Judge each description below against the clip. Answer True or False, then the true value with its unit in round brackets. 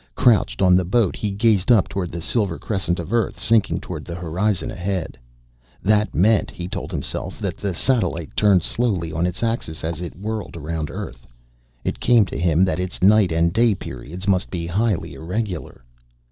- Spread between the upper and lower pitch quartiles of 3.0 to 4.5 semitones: True (4.1 semitones)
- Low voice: True (95 Hz)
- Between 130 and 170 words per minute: False (185 wpm)